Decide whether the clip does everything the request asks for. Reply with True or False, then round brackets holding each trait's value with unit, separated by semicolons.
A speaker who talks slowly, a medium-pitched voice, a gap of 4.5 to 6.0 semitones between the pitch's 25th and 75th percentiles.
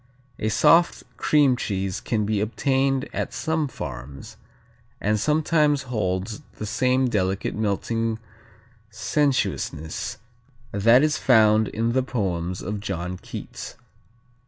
False (110 wpm; 110 Hz; 5.1 semitones)